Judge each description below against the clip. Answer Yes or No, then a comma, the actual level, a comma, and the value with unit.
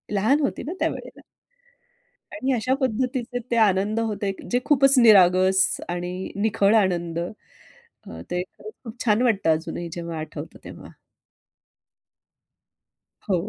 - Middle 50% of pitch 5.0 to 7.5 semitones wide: Yes, wide, 5.4 semitones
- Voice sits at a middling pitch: No, high, 210 Hz